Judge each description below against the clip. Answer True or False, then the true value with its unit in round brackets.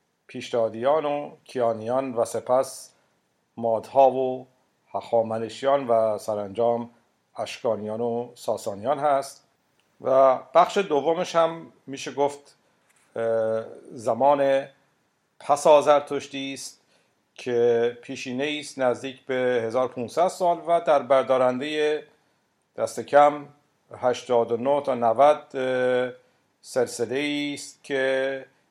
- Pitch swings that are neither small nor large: True (3.1 semitones)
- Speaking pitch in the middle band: False (130 Hz)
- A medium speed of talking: False (90 wpm)